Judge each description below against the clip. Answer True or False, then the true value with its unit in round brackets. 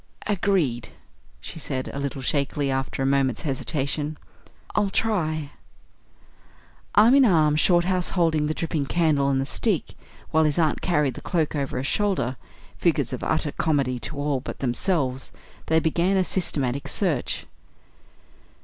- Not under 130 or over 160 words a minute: True (150 wpm)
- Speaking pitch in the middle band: True (150 Hz)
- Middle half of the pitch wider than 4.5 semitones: False (4.2 semitones)